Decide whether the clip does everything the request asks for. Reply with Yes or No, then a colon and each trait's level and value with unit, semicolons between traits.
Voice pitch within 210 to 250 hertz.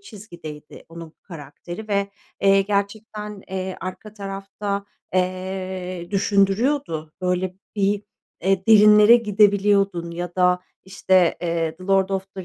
No: high, 195 Hz